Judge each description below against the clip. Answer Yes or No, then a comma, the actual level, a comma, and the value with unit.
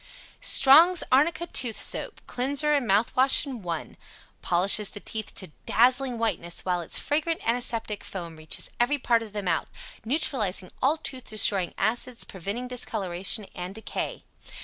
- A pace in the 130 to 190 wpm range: Yes, average, 150 wpm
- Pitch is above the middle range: Yes, high, 230 Hz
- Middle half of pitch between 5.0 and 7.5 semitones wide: Yes, wide, 5.5 semitones